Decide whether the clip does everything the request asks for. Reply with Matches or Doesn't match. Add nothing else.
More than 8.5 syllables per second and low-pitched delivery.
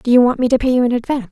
Doesn't match